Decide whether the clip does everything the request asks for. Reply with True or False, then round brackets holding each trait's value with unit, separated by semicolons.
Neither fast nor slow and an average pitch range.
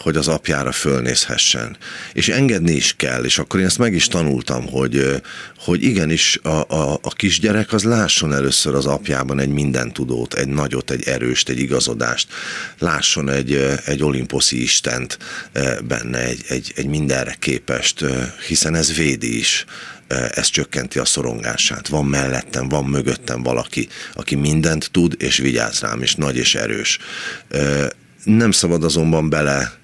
True (145 wpm; 3.2 semitones)